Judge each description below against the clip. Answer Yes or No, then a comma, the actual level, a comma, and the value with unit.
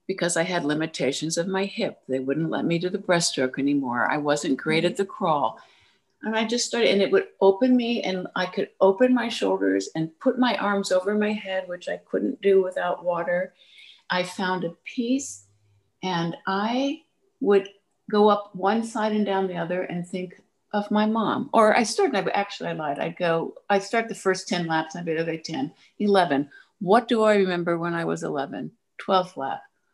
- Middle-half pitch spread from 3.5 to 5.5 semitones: Yes, average, 4.0 semitones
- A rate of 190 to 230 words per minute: Yes, average, 200 wpm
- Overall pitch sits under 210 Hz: Yes, medium, 185 Hz